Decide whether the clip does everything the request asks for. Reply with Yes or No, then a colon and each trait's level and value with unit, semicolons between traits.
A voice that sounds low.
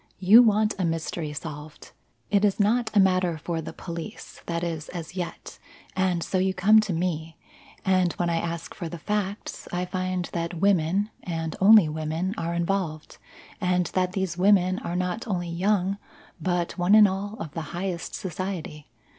No: medium, 180 Hz